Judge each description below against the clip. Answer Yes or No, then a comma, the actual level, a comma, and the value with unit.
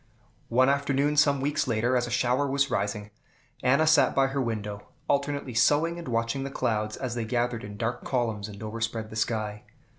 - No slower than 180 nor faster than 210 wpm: Yes, average, 185 wpm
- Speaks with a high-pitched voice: No, low, 120 Hz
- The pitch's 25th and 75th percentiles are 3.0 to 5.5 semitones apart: Yes, average, 4.0 semitones